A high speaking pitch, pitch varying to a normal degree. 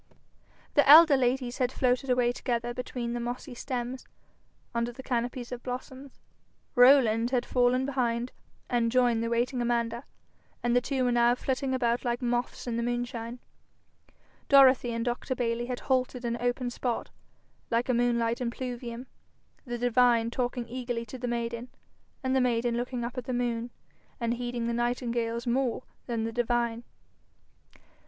No: high, 245 Hz; narrow, 1.1 semitones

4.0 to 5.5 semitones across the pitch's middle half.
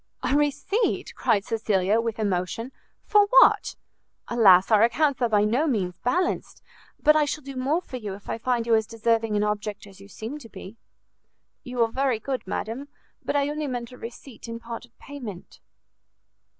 Yes: average, 4.5 semitones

